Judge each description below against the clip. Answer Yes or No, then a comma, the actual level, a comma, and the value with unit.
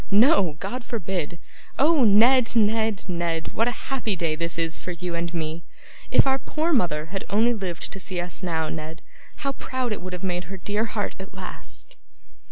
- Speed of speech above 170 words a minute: Yes, average, 190 wpm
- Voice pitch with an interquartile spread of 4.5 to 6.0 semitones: Yes, average, 5.2 semitones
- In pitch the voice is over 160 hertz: Yes, high, 190 Hz